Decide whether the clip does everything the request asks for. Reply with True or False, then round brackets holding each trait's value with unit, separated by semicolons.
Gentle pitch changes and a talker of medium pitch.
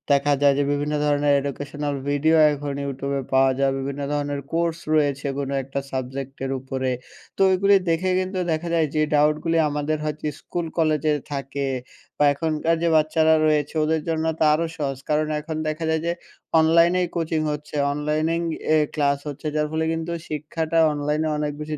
True (2.1 semitones; 150 Hz)